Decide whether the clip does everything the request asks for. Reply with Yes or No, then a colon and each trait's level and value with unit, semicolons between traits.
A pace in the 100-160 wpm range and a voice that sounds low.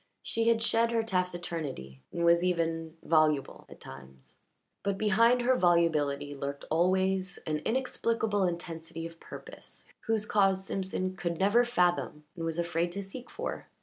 No: average, 150 wpm; medium, 175 Hz